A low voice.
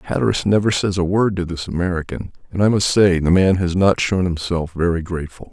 Yes: very low, 90 Hz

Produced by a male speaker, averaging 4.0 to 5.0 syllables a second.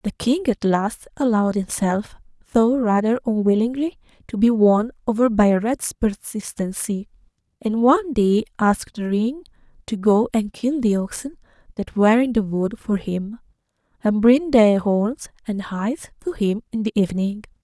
No: female; 4.6 syllables/s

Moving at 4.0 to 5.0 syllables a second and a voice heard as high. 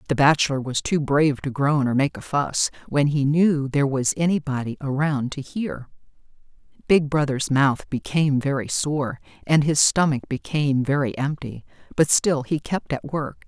No: 4.8 syllables/s; medium, 140 Hz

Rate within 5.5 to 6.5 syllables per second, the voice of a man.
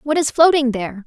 No: 5.8 syllables/s; female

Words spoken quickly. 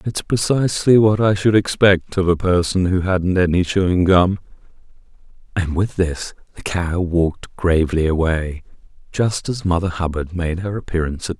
No: average, 170 wpm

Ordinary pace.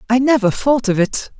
No: fast, 215 wpm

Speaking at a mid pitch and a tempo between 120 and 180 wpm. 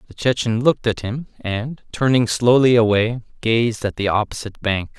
No: low, 115 Hz; average, 170 wpm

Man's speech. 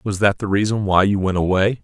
Yes: male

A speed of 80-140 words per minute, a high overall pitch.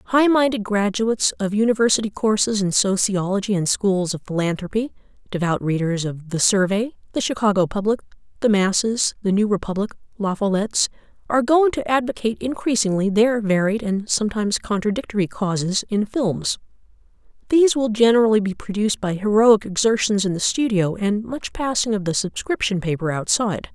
No: average, 150 wpm; high, 210 Hz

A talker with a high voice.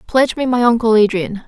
Yes: high, 230 Hz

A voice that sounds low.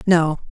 No: medium, 165 Hz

